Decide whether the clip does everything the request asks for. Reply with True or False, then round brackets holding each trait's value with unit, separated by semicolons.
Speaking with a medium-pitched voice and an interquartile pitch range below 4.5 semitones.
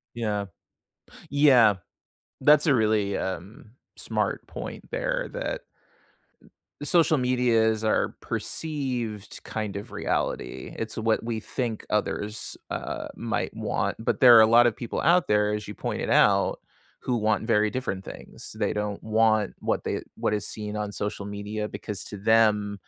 False (110 Hz; 2.8 semitones)